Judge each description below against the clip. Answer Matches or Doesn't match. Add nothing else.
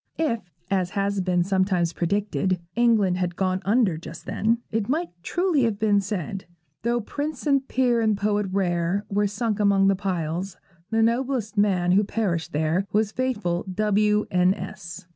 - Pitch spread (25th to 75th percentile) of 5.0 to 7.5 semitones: Doesn't match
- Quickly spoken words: Doesn't match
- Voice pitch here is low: Doesn't match